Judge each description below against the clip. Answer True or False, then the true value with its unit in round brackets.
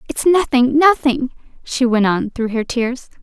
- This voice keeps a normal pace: True (165 wpm)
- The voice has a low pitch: False (260 Hz)